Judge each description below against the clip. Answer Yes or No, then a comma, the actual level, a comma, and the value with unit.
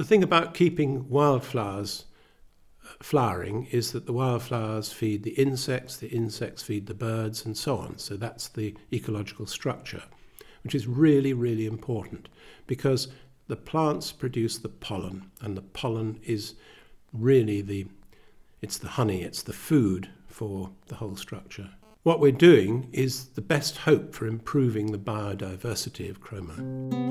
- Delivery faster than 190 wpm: No, average, 145 wpm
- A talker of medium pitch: No, low, 115 Hz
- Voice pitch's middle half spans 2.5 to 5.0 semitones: Yes, average, 3.9 semitones